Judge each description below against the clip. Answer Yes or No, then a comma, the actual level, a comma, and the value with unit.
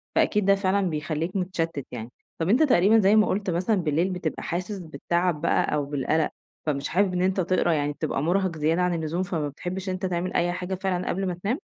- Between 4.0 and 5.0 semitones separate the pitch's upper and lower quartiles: No, average, 3.1 semitones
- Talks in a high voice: No, medium, 180 Hz